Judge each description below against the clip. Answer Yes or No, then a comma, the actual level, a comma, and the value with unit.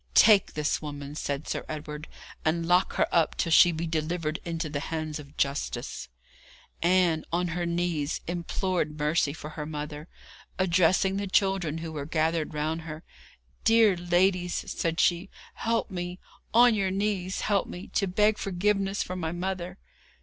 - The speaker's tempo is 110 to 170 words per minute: Yes, average, 155 wpm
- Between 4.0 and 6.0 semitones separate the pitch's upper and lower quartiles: No, average, 3.3 semitones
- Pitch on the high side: No, medium, 170 Hz